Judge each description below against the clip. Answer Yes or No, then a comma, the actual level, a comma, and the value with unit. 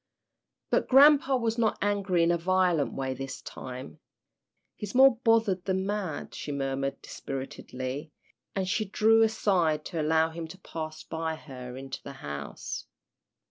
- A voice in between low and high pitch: Yes, medium, 165 Hz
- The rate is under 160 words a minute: Yes, average, 145 wpm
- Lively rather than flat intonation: Yes, wide, 6.9 semitones